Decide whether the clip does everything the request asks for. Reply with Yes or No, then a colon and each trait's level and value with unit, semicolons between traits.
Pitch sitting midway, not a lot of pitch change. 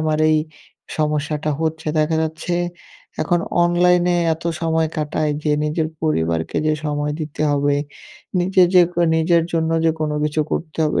Yes: medium, 155 Hz; narrow, 1.5 semitones